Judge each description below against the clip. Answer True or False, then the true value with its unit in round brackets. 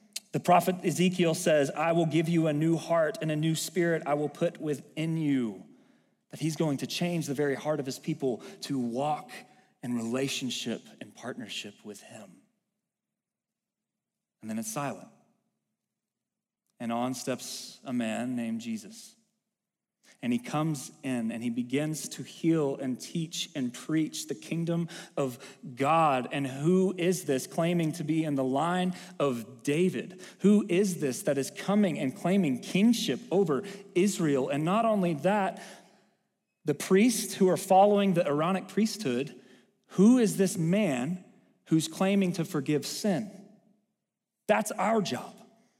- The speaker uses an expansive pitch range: True (5.7 semitones)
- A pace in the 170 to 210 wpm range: False (150 wpm)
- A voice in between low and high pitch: True (175 Hz)